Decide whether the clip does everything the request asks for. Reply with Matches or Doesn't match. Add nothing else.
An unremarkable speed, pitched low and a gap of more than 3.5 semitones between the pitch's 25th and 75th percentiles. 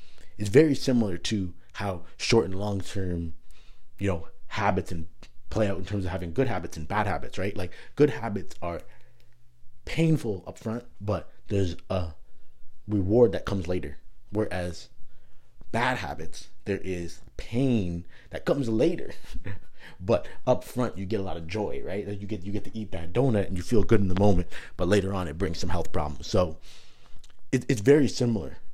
Matches